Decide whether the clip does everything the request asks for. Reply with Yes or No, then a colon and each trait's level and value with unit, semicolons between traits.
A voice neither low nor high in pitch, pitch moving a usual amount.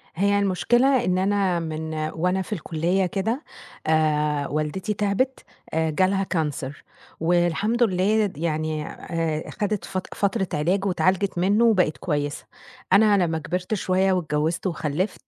Yes: medium, 180 Hz; average, 4.1 semitones